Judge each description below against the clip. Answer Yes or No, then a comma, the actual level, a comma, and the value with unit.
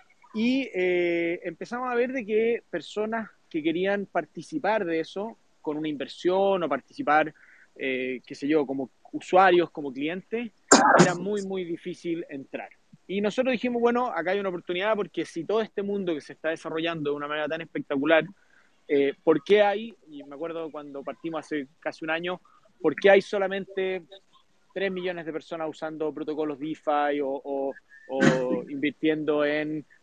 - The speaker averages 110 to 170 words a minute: Yes, average, 165 wpm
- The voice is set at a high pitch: No, medium, 170 Hz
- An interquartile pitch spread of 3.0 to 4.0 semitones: No, average, 4.6 semitones